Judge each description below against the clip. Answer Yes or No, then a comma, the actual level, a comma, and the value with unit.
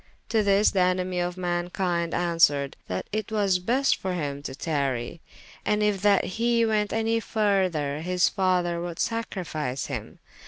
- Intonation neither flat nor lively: Yes, average, 3.8 semitones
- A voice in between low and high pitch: Yes, medium, 180 Hz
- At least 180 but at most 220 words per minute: No, average, 155 wpm